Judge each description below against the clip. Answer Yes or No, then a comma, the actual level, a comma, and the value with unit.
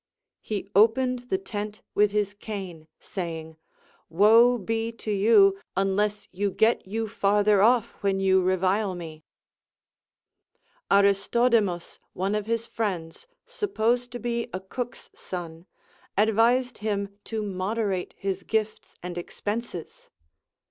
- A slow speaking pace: Yes, slow, 120 wpm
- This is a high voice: Yes, high, 205 Hz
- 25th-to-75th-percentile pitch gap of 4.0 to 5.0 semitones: No, average, 3.1 semitones